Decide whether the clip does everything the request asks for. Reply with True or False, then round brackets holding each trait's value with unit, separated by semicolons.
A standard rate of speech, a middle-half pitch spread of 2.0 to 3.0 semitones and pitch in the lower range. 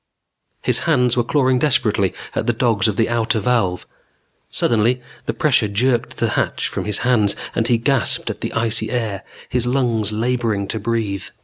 True (175 wpm; 2.7 semitones; 115 Hz)